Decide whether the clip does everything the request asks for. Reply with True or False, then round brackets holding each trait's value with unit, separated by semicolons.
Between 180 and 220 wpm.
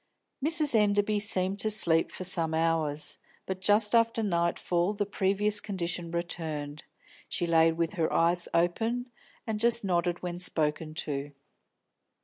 False (135 wpm)